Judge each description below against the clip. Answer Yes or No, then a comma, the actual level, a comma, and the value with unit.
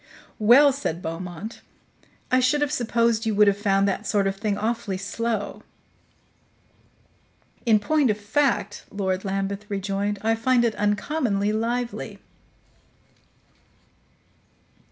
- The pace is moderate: No, slow, 115 wpm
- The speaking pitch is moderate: No, high, 210 Hz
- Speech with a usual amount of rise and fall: Yes, average, 3.0 semitones